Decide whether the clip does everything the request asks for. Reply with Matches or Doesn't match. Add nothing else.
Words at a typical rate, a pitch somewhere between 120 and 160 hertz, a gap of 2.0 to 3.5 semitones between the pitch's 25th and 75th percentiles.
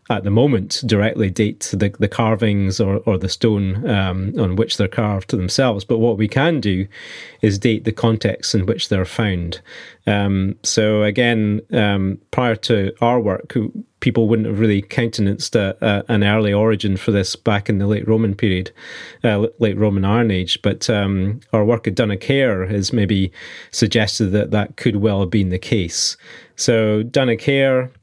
Doesn't match